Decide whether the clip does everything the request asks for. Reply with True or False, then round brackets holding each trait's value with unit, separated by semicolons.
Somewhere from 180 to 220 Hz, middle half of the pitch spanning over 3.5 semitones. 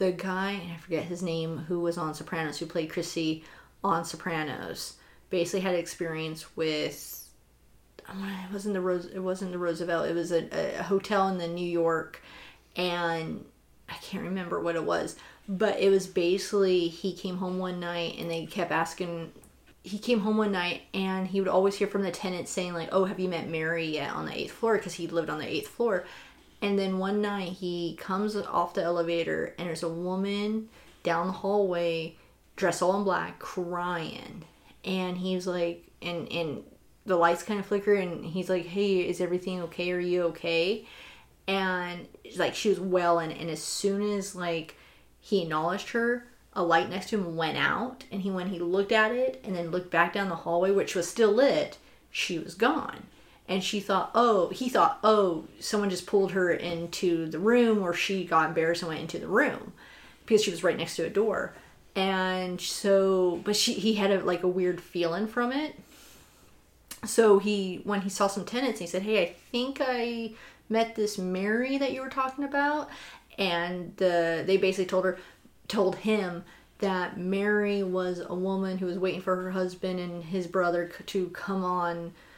False (185 Hz; 2.7 semitones)